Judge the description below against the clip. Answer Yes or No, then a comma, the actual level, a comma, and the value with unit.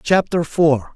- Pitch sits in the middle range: Yes, medium, 160 Hz